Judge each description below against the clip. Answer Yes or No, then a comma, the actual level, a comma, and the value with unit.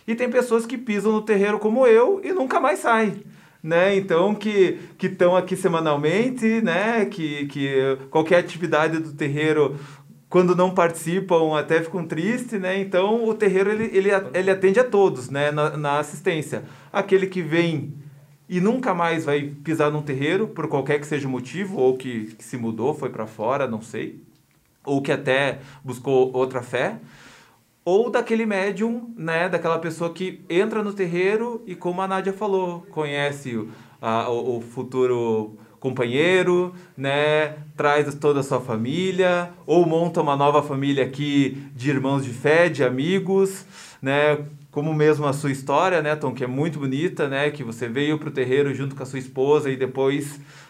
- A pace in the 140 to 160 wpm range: No, average, 170 wpm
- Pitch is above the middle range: No, medium, 155 Hz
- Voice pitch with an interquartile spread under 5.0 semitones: No, average, 5.3 semitones